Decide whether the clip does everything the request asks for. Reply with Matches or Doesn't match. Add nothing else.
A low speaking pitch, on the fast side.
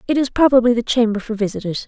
Doesn't match